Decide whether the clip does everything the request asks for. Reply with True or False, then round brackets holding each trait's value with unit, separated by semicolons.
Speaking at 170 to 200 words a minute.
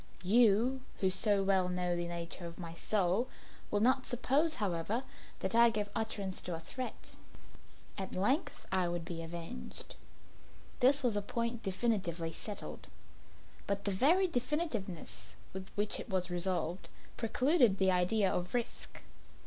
False (145 wpm)